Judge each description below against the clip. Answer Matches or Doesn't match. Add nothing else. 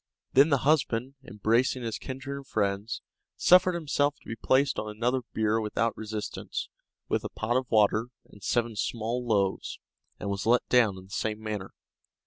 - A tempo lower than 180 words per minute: Matches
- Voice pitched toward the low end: Matches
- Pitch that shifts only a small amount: Doesn't match